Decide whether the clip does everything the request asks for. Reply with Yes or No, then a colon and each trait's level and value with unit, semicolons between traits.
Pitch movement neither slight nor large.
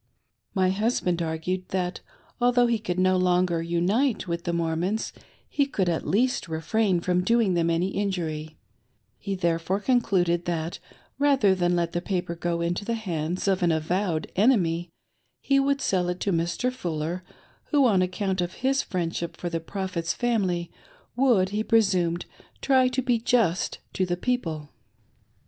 Yes: average, 4.3 semitones